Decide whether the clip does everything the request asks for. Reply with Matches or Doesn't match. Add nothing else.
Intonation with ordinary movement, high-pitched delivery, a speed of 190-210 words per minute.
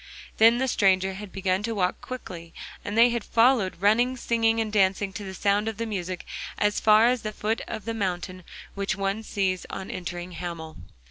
Matches